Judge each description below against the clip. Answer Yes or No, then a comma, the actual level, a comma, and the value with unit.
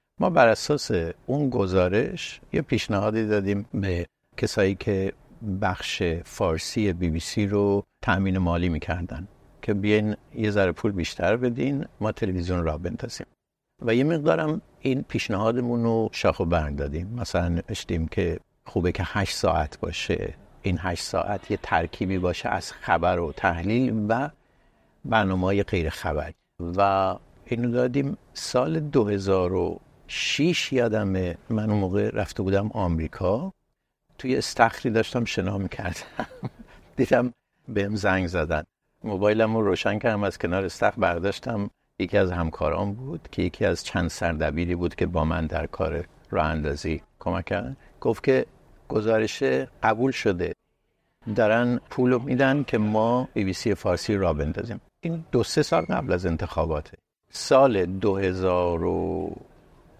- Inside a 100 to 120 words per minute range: No, average, 135 wpm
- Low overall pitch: Yes, low, 100 Hz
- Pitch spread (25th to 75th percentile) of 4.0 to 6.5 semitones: Yes, average, 4.6 semitones